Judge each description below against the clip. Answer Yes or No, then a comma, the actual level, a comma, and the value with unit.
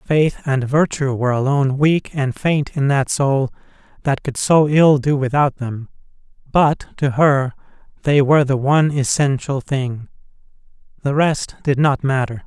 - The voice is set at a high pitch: No, medium, 140 Hz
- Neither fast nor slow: Yes, average, 155 wpm